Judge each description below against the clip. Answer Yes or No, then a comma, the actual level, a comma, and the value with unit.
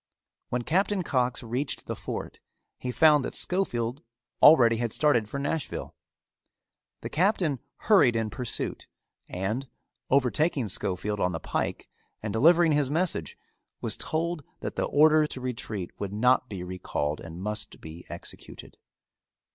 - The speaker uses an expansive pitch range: Yes, wide, 6.4 semitones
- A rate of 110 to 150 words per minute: Yes, average, 140 wpm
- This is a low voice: Yes, low, 125 Hz